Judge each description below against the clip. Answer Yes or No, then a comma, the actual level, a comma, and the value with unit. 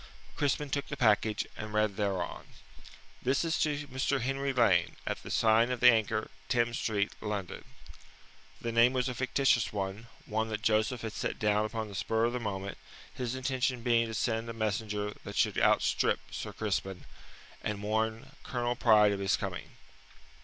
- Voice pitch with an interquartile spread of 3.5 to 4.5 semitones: No, average, 2.8 semitones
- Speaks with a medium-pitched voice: No, low, 110 Hz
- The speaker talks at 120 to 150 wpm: No, average, 175 wpm